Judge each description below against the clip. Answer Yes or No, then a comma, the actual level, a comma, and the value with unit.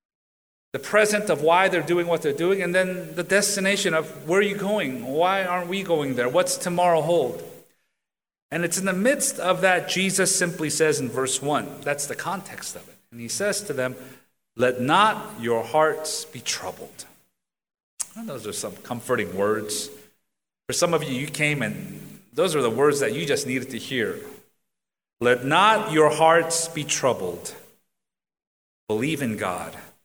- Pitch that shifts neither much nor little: No, wide, 6.0 semitones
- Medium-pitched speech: Yes, medium, 165 Hz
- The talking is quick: No, average, 175 wpm